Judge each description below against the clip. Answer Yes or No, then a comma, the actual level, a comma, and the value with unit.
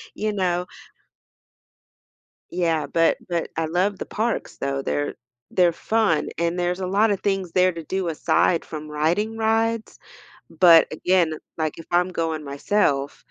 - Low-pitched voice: No, medium, 175 Hz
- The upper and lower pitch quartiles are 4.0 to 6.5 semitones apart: No, average, 3.3 semitones